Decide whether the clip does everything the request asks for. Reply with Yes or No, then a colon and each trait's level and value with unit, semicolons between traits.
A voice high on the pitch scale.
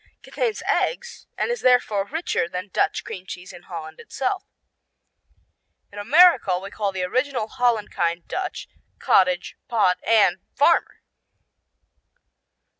Yes: high, 205 Hz